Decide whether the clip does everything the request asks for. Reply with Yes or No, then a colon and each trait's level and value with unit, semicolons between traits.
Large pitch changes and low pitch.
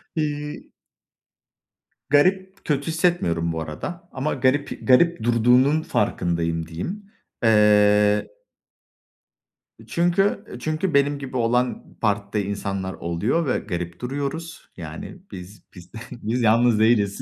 Yes: wide, 7.3 semitones; low, 120 Hz